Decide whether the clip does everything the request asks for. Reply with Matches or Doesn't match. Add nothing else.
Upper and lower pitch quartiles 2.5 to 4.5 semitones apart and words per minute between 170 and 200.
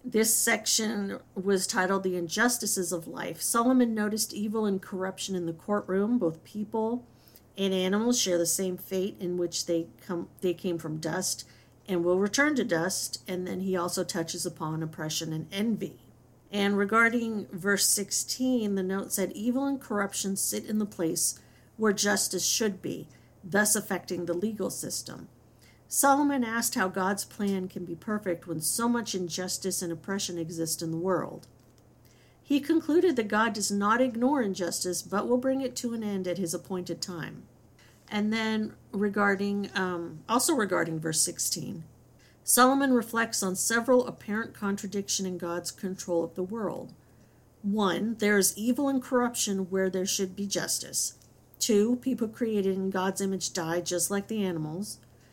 Doesn't match